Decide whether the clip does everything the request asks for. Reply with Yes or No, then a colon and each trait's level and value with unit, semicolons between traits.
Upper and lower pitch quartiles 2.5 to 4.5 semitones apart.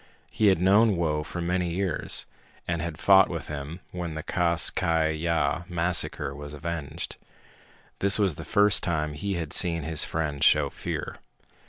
Yes: average, 2.9 semitones